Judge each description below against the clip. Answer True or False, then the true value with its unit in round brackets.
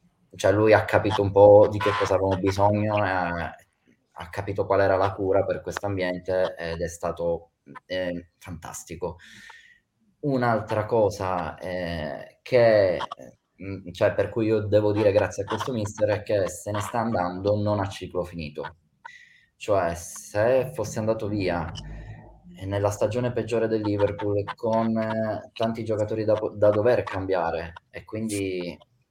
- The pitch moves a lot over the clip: False (3.0 semitones)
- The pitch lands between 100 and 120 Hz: True (105 Hz)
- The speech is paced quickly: False (145 wpm)